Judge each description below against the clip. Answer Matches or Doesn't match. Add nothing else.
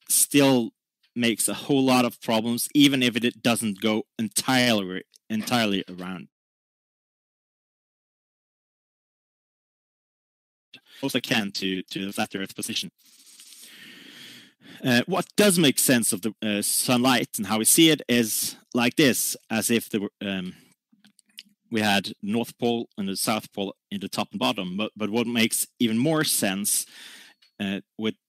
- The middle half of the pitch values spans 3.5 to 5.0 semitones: Matches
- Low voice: Matches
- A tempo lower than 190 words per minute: Matches